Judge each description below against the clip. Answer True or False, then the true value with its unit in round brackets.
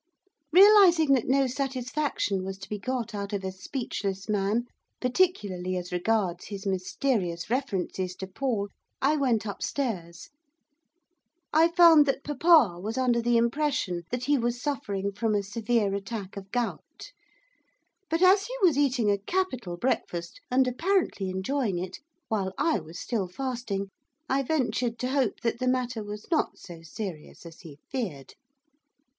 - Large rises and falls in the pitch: True (5.8 semitones)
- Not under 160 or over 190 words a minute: False (150 wpm)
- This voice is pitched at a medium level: False (230 Hz)